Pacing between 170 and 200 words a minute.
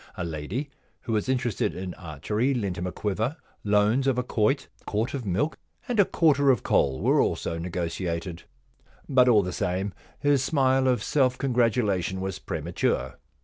Yes: average, 175 wpm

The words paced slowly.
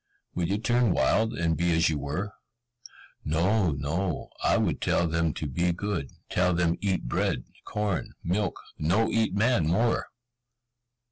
No: average, 150 wpm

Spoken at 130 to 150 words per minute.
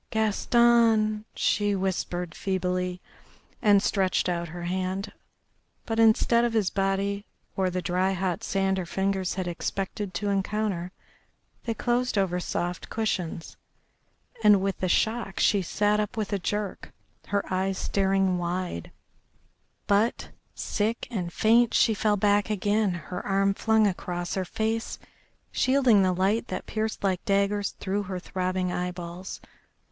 Yes: average, 140 wpm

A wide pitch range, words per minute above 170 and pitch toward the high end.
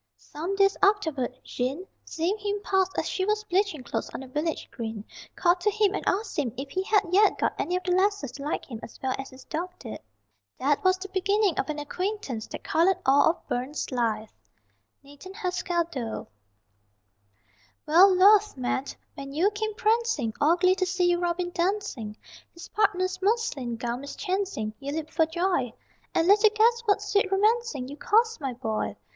Yes: wide, 6.5 semitones; average, 185 wpm; very high, 355 Hz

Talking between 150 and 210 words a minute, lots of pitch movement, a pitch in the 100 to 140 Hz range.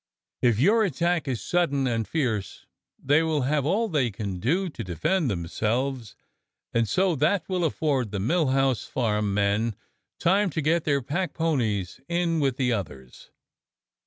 Yes: average, 160 wpm; wide, 6.8 semitones; low, 135 Hz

